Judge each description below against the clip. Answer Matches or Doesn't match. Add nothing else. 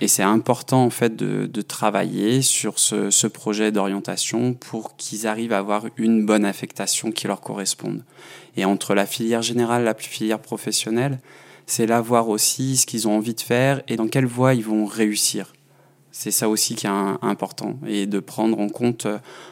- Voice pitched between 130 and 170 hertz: Doesn't match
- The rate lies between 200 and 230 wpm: Doesn't match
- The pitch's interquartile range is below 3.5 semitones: Matches